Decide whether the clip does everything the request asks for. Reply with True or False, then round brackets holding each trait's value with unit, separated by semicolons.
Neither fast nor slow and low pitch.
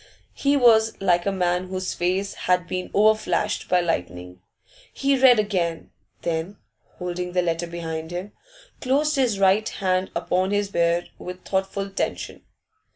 False (145 wpm; 185 Hz)